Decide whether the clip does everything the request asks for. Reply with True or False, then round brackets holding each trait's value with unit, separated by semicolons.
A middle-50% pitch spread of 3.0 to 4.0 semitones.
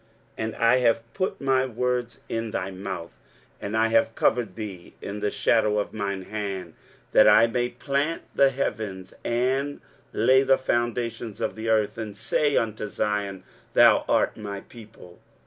True (3.3 semitones)